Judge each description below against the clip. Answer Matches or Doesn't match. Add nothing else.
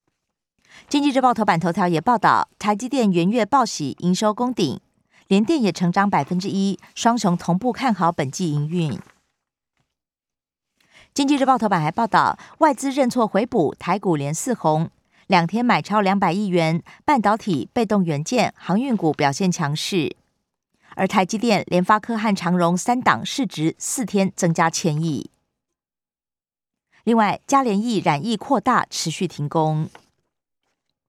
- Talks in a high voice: Matches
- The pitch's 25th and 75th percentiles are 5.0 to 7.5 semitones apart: Matches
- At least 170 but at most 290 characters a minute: Matches